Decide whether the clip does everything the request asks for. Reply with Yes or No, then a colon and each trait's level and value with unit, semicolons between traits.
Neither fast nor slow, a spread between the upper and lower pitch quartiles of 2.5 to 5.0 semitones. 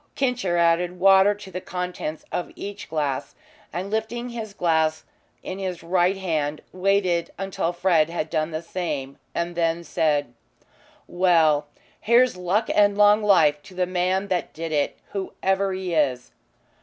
Yes: average, 150 wpm; average, 3.3 semitones